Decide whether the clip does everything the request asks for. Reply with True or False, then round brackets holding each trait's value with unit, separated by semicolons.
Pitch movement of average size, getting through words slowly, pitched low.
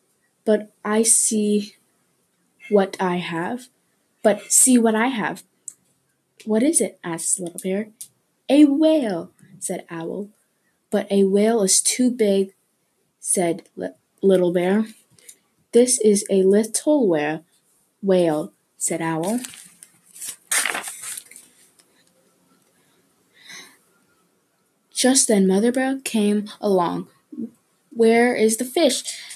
False (3.8 semitones; 100 wpm; 210 Hz)